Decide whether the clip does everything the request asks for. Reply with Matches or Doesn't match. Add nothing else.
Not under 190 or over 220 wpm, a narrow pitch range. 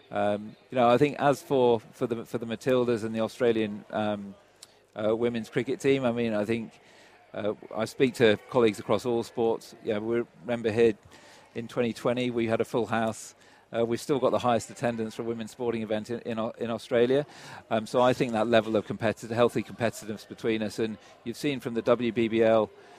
Matches